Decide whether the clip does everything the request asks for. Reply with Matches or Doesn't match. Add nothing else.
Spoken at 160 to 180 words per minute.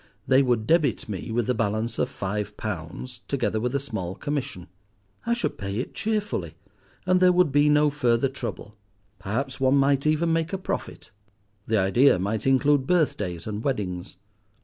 Matches